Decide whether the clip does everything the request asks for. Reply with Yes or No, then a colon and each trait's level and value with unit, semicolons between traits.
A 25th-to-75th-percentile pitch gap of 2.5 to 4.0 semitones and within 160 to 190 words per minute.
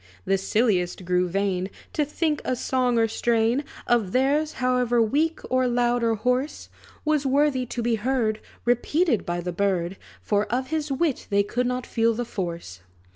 No: average, 4.5 semitones; average, 170 wpm